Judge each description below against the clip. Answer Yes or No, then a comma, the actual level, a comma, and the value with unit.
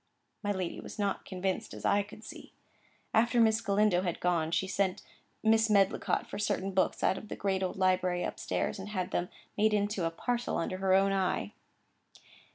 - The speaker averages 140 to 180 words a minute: No, average, 195 wpm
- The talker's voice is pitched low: No, high, 195 Hz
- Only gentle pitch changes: Yes, narrow, 2.2 semitones